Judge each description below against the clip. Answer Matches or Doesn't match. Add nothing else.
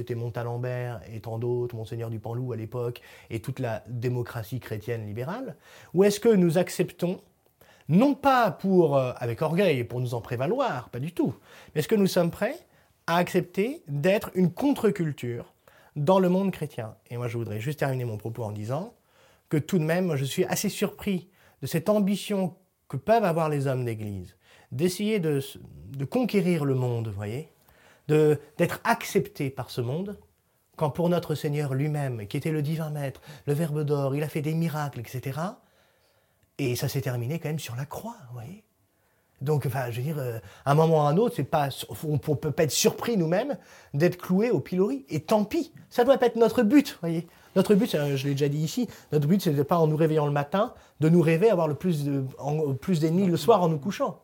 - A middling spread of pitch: Doesn't match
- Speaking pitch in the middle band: Matches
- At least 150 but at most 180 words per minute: Doesn't match